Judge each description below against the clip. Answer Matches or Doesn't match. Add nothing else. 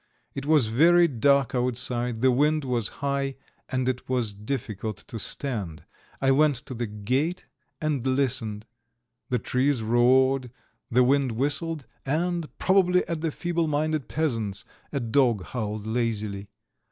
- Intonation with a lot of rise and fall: Doesn't match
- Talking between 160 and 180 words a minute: Doesn't match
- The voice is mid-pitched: Doesn't match